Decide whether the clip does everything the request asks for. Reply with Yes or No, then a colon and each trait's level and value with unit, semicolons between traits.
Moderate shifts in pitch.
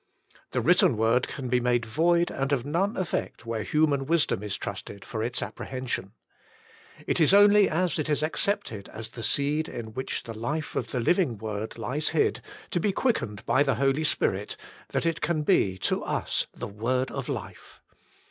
No: wide, 5.7 semitones